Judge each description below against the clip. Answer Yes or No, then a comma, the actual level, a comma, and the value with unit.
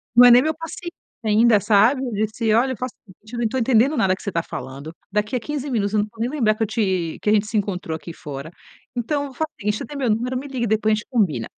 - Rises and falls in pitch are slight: No, average, 3.8 semitones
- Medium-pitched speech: No, high, 220 Hz